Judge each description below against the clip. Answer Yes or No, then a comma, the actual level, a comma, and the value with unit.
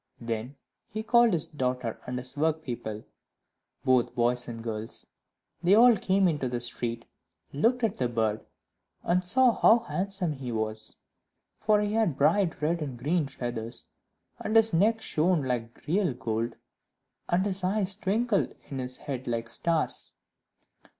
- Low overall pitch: No, medium, 150 Hz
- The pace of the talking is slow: No, average, 150 wpm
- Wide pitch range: Yes, wide, 8.4 semitones